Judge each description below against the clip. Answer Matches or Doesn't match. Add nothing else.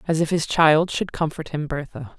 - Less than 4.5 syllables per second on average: Doesn't match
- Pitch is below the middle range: Doesn't match